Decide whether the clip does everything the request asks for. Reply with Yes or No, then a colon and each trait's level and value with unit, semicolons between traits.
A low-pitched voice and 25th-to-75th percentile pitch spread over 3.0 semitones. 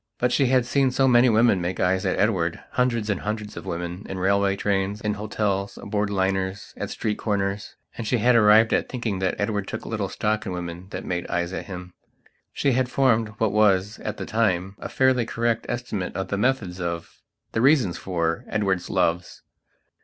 Yes: low, 105 Hz; average, 3.4 semitones